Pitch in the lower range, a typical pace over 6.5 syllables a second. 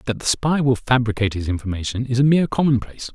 Yes: low, 120 Hz; 7.0 syllables/s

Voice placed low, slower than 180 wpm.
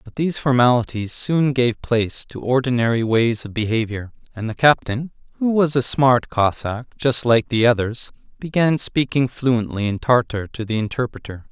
Yes: low, 125 Hz; average, 160 wpm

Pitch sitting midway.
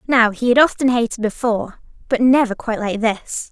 No: high, 235 Hz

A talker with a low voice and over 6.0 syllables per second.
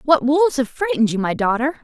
No: very high, 265 Hz; 6.6 syllables/s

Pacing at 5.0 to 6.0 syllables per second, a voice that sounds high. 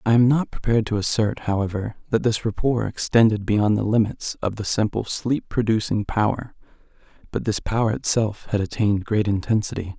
No: 5.4 syllables/s; low, 110 Hz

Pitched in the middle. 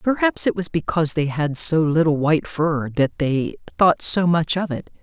Yes: medium, 160 Hz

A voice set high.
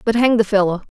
Yes: high, 215 Hz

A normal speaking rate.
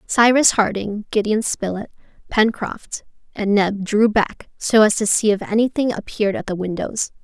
Yes: average, 160 wpm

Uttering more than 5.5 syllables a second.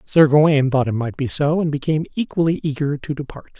Yes: 6.0 syllables/s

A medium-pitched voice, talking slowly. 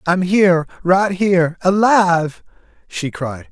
Yes: medium, 175 Hz; slow, 100 wpm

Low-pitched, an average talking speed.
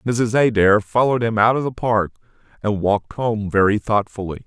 Yes: low, 110 Hz; average, 175 wpm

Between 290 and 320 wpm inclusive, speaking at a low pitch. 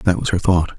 Yes: fast, 305 wpm; very low, 90 Hz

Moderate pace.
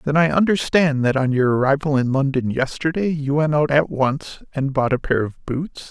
No: fast, 215 wpm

